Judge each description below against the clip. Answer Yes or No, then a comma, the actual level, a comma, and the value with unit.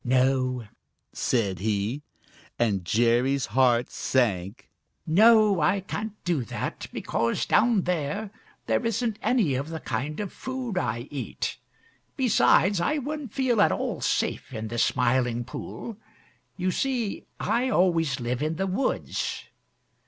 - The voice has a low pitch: No, medium, 155 Hz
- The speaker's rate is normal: No, slow, 130 wpm